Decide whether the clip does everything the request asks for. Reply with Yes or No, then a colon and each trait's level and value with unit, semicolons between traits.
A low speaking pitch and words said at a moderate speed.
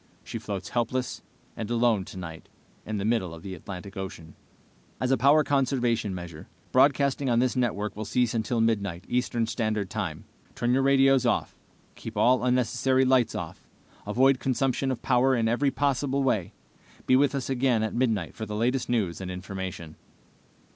Yes: low, 120 Hz; average, 170 wpm